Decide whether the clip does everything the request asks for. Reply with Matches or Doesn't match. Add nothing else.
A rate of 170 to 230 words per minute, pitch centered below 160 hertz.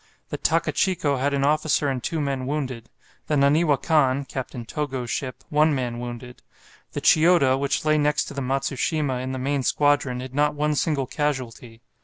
Matches